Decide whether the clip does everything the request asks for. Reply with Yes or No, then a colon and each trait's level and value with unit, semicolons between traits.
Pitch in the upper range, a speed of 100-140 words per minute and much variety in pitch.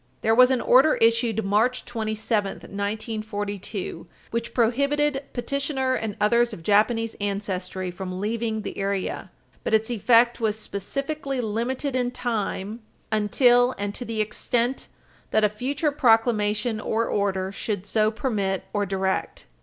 No: high, 220 Hz; slow, 135 wpm; average, 3.1 semitones